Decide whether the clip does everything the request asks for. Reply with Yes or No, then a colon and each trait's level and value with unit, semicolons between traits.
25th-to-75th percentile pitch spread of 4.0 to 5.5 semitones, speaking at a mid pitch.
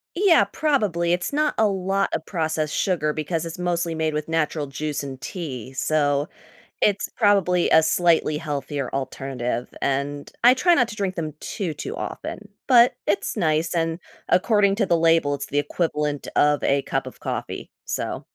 Yes: average, 4.9 semitones; medium, 165 Hz